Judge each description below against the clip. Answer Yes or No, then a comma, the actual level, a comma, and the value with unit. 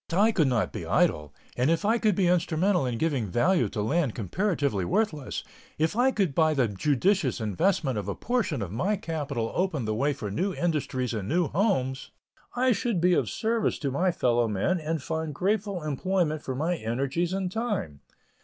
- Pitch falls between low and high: Yes, medium, 160 Hz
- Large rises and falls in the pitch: Yes, wide, 6.9 semitones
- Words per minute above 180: Yes, average, 190 wpm